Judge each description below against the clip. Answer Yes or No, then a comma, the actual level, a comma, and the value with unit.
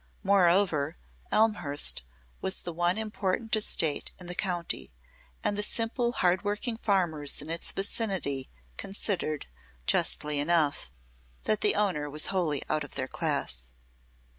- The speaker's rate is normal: No, slow, 130 wpm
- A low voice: No, medium, 180 Hz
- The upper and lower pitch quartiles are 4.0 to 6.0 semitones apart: Yes, wide, 5.4 semitones